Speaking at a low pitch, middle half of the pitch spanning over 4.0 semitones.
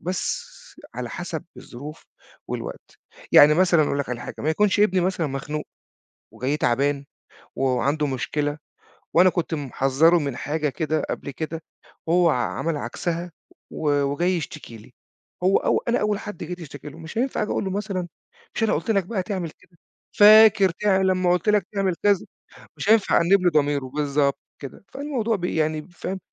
No: medium, 165 Hz; average, 4.7 semitones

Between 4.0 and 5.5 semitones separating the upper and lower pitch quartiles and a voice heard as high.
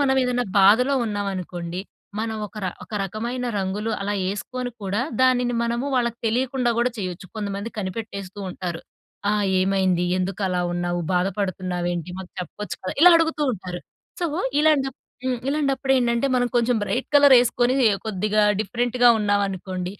Yes: average, 4.8 semitones; high, 210 Hz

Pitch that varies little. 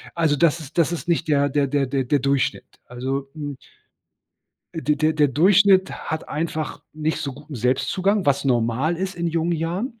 No: average, 3.3 semitones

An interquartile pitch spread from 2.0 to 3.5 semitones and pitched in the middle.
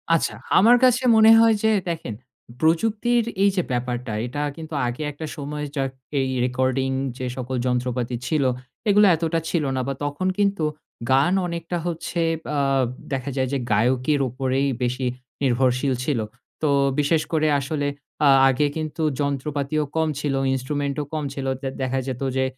No: average, 3.9 semitones; medium, 145 Hz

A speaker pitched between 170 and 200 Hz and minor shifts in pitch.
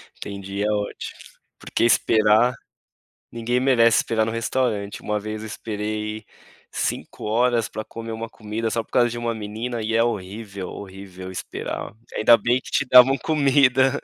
No: low, 110 Hz; narrow, 2.2 semitones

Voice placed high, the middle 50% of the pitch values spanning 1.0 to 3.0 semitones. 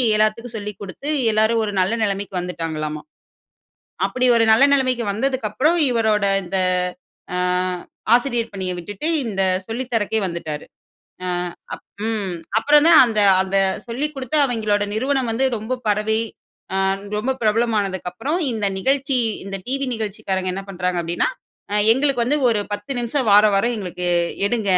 No: high, 220 Hz; average, 4.4 semitones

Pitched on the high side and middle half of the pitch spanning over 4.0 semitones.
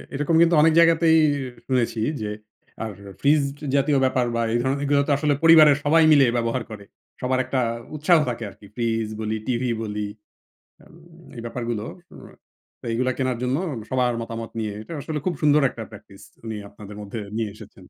No: low, 125 Hz; average, 4.5 semitones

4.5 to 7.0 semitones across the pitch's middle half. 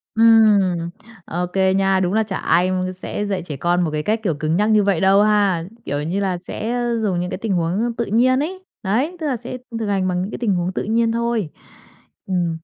No: average, 3.8 semitones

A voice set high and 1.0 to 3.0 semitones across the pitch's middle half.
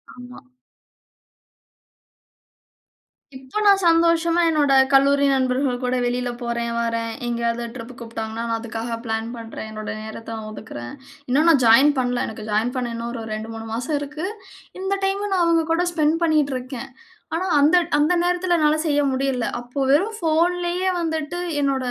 No: very high, 260 Hz; wide, 5.6 semitones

